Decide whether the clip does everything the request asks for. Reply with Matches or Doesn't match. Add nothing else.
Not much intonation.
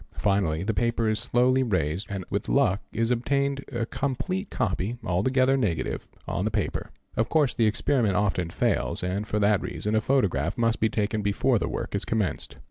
Doesn't match